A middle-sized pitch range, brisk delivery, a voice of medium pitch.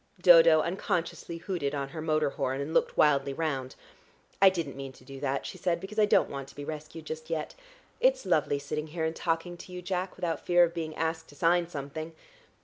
Yes: average, 3.4 semitones; fast, 215 wpm; medium, 160 Hz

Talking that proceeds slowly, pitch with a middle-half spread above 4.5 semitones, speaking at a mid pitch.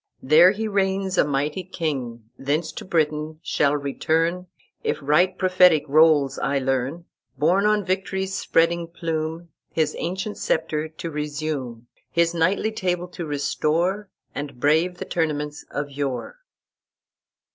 No: slow, 130 wpm; average, 3.7 semitones; medium, 160 Hz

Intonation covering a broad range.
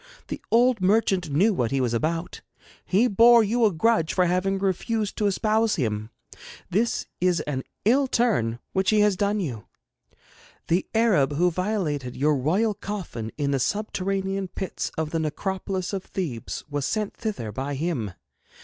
Yes: wide, 6.3 semitones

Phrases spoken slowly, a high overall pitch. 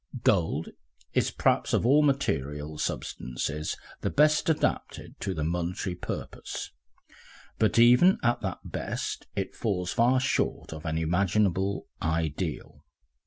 No: slow, 120 wpm; very low, 90 Hz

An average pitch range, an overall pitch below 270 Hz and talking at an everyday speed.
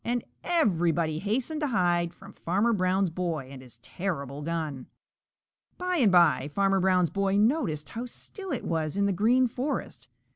No: wide, 6.1 semitones; high, 190 Hz; average, 160 wpm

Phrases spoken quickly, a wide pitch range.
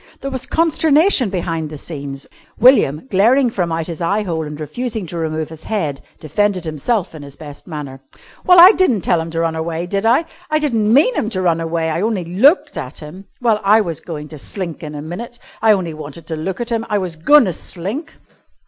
Yes: fast, 220 wpm; wide, 6.2 semitones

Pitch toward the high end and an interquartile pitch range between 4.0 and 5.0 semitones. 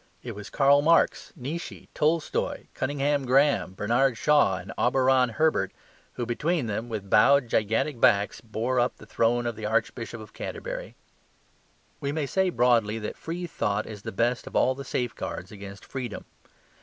No: low, 125 Hz; average, 4.6 semitones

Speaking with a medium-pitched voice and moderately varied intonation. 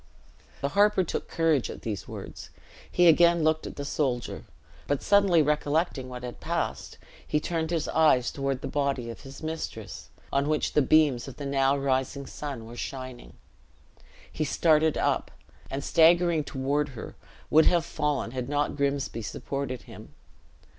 Yes: medium, 145 Hz; average, 3.1 semitones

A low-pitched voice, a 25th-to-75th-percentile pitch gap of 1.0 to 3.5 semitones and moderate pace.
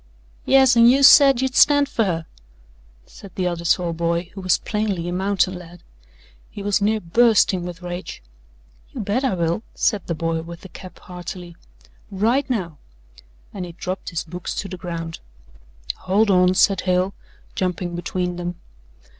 No: medium, 185 Hz; average, 3.2 semitones; average, 165 wpm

